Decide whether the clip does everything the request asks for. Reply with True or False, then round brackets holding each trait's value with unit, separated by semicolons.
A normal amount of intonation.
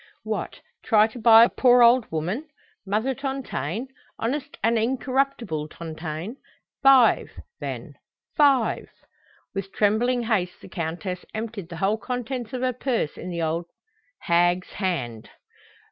False (6.2 semitones)